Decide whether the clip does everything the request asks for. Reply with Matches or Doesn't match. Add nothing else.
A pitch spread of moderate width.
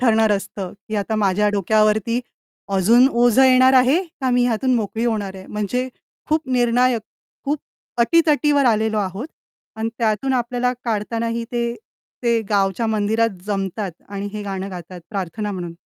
Matches